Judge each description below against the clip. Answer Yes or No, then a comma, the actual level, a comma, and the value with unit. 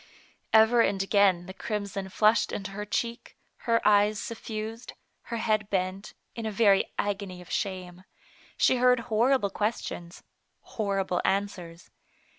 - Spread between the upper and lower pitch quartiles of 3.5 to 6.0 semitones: No, narrow, 2.5 semitones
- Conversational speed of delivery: No, slow, 130 wpm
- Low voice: No, high, 205 Hz